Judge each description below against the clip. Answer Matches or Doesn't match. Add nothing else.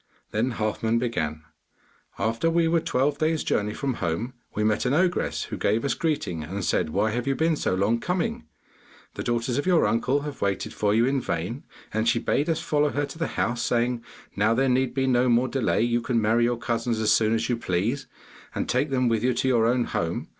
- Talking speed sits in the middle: Doesn't match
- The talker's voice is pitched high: Doesn't match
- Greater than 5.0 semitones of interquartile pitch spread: Doesn't match